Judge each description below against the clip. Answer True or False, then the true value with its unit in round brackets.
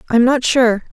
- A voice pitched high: True (240 Hz)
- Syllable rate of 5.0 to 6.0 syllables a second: True (5.8 syllables/s)